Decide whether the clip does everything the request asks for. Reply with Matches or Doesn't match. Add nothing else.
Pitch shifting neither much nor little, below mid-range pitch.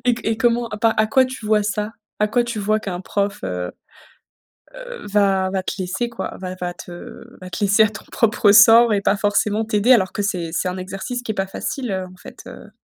Doesn't match